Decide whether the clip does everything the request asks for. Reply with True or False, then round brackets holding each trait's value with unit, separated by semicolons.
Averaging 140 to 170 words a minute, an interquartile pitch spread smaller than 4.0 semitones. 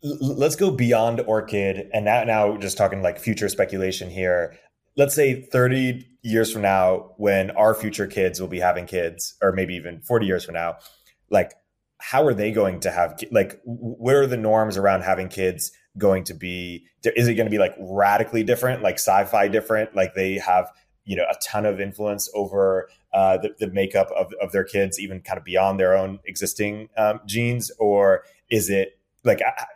False (190 wpm; 2.9 semitones)